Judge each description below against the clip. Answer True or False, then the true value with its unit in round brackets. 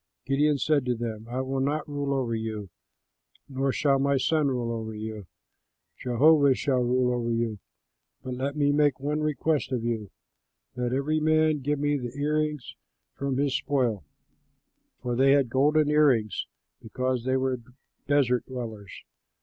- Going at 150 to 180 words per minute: True (160 wpm)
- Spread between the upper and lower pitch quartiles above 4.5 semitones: False (3.2 semitones)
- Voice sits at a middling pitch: False (130 Hz)